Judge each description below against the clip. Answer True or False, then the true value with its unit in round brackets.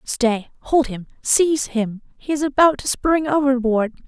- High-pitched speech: True (260 Hz)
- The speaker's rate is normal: False (120 wpm)